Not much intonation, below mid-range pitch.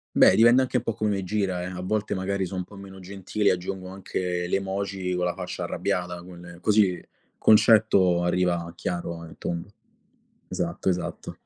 Yes: narrow, 2.1 semitones; very low, 95 Hz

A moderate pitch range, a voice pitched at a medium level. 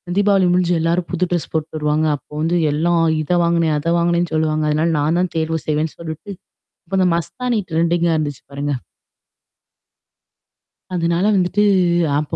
No: narrow, 2.1 semitones; medium, 170 Hz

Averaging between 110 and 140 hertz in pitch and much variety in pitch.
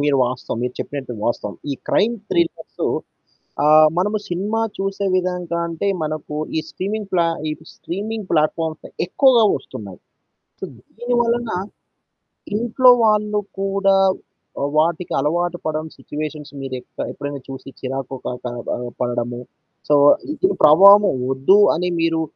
No: medium, 170 Hz; wide, 6.0 semitones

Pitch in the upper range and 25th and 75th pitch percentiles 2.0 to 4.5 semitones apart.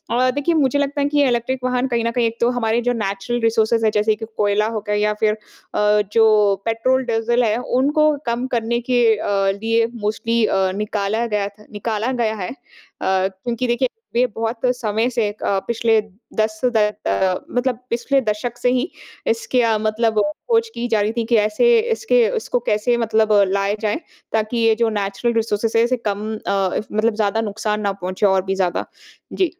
Yes: high, 225 Hz; narrow, 2.5 semitones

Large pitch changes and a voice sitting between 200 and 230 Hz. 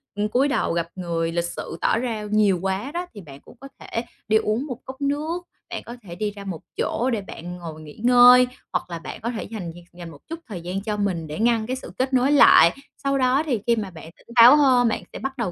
Yes: wide, 6.2 semitones; high, 220 Hz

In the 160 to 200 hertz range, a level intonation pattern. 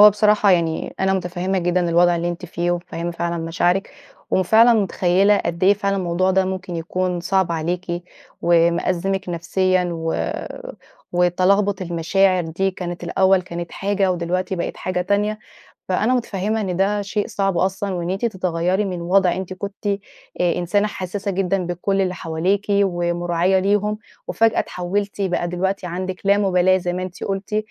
Yes: medium, 185 Hz; narrow, 2.0 semitones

